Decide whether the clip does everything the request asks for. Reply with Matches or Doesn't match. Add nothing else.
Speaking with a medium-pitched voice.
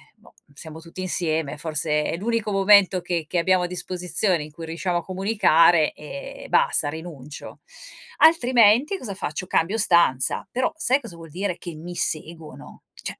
Matches